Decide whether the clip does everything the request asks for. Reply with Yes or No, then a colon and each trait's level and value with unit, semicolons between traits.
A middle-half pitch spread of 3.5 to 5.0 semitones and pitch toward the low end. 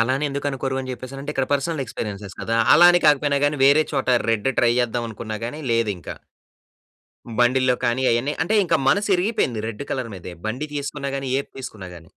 Yes: average, 3.8 semitones; low, 130 Hz